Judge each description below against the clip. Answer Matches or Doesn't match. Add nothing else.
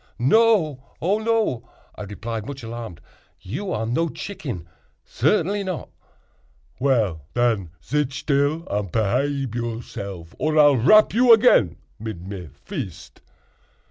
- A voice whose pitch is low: Matches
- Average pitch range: Doesn't match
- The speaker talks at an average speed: Doesn't match